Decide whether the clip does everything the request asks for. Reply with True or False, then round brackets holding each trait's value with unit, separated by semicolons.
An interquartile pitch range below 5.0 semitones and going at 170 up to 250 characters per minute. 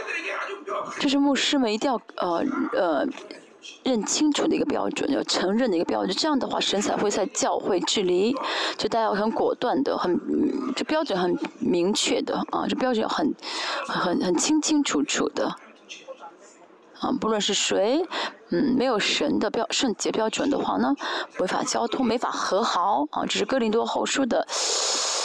True (4.0 semitones; 240 characters per minute)